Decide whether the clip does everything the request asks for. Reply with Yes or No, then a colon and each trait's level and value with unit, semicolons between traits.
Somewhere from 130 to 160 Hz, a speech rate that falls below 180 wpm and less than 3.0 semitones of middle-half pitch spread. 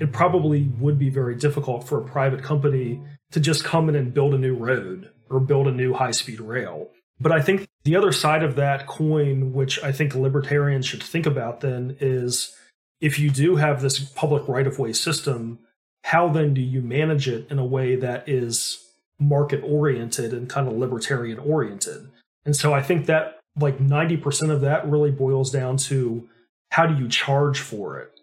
No: medium, 140 Hz; average, 195 wpm; narrow, 2.6 semitones